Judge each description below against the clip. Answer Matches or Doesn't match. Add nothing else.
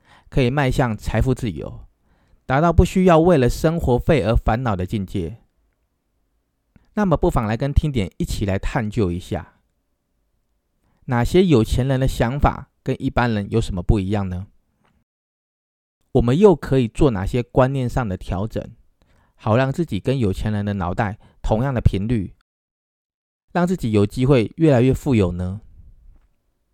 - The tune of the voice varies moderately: Doesn't match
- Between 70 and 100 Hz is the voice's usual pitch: Doesn't match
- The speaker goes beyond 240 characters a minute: Doesn't match